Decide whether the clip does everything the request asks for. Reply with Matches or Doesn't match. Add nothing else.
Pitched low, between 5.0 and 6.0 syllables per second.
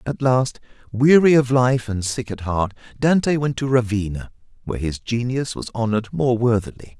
Matches